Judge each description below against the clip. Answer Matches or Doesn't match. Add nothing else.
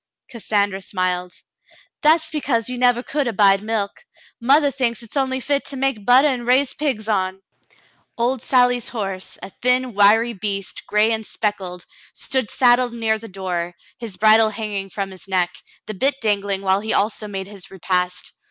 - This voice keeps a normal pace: Matches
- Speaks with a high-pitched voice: Matches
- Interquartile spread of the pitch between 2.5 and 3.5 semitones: Doesn't match